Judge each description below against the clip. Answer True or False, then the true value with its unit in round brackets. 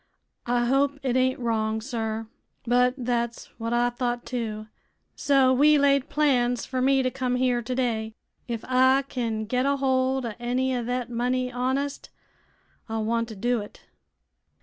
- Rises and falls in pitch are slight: True (1.8 semitones)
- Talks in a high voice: True (250 Hz)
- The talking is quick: False (160 wpm)